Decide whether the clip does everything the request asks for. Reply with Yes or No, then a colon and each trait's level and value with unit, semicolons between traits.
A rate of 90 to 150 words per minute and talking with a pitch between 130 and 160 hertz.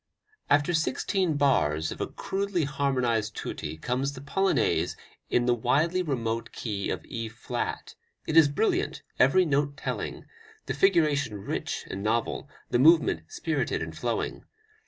Yes: average, 140 wpm; medium, 140 Hz